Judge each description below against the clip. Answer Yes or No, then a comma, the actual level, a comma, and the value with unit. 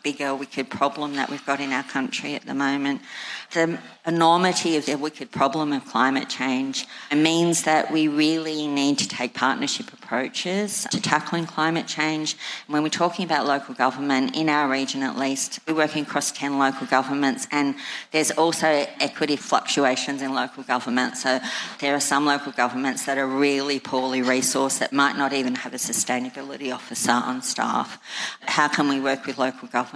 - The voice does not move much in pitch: Yes, narrow, 2.3 semitones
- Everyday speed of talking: Yes, average, 175 wpm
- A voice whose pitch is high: No, medium, 140 Hz